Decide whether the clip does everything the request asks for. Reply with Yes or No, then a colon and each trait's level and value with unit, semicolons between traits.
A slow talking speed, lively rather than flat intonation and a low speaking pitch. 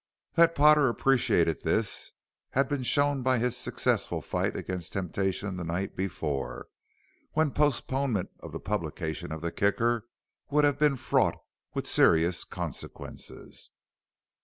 Yes: slow, 130 wpm; wide, 7.8 semitones; low, 115 Hz